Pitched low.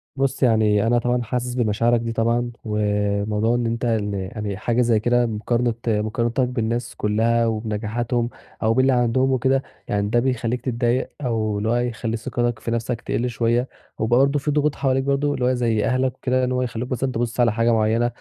Yes: low, 120 Hz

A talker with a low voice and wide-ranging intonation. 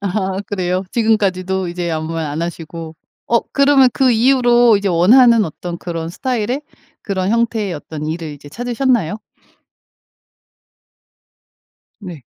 No: high, 190 Hz; wide, 5.8 semitones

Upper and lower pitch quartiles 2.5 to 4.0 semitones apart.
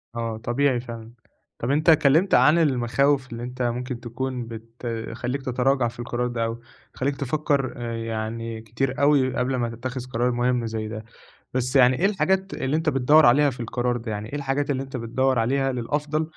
Yes: average, 2.9 semitones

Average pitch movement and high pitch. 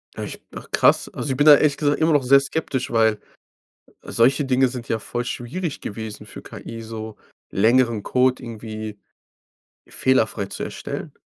No: average, 3.6 semitones; low, 125 Hz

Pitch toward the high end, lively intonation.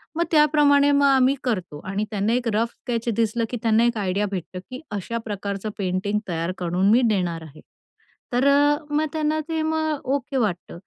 Yes: high, 230 Hz; wide, 6.3 semitones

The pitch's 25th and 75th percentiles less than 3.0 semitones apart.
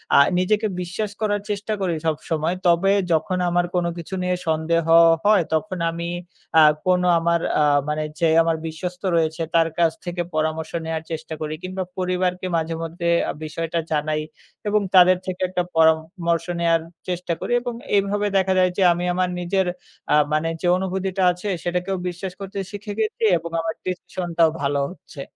Yes: narrow, 2.4 semitones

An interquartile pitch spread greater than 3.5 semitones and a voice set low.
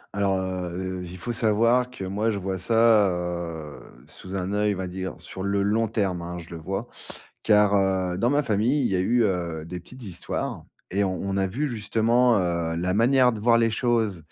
Yes: average, 3.9 semitones; low, 100 Hz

